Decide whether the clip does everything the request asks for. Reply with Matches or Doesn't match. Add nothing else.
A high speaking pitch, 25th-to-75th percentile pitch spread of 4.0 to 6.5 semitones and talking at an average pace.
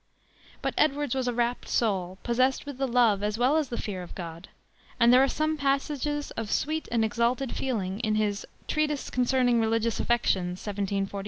Matches